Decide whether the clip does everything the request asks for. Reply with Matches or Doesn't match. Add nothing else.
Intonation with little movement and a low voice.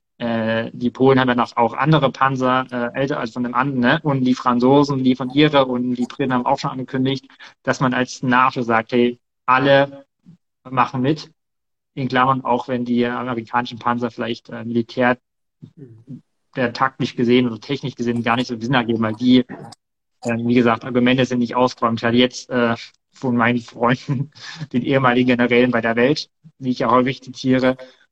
Matches